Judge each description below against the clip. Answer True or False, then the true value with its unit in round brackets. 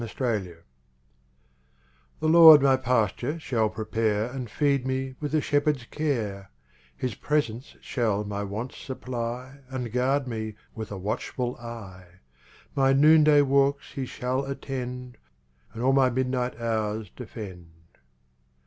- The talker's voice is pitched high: False (125 Hz)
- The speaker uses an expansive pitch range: False (3.7 semitones)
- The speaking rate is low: True (130 wpm)